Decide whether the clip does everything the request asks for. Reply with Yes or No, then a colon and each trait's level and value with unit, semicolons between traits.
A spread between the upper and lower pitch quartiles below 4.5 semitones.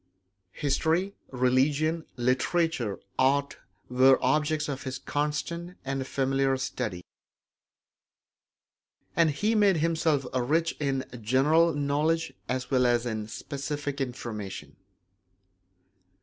Yes: average, 3.6 semitones